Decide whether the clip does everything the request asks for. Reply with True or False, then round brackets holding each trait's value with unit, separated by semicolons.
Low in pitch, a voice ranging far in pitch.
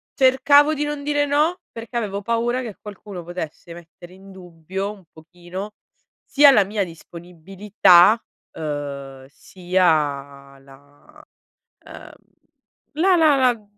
False (190 Hz; 6.8 semitones)